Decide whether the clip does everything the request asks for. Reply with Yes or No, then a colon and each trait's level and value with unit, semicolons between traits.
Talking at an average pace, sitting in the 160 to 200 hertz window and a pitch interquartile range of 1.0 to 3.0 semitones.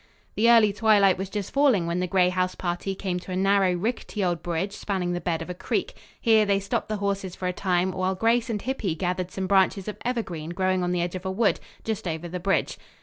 No: fast, 240 wpm; high, 190 Hz; narrow, 2.4 semitones